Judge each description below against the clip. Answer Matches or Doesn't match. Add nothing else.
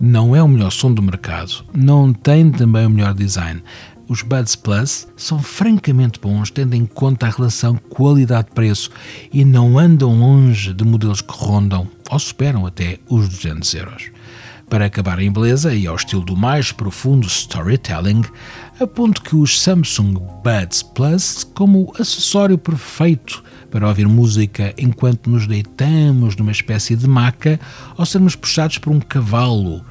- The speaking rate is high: Doesn't match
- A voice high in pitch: Doesn't match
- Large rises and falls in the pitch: Doesn't match